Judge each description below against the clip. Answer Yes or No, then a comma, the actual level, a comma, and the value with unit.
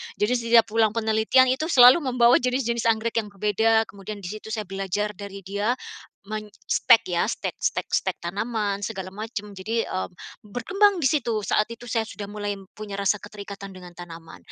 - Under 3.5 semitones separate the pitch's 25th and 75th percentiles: Yes, narrow, 2.6 semitones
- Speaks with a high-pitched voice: Yes, high, 215 Hz